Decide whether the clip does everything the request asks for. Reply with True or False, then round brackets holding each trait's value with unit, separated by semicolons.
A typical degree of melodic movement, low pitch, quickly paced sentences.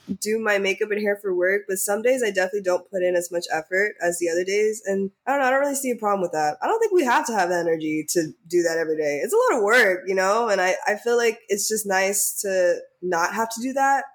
False (4.1 semitones; 195 Hz; 295 wpm)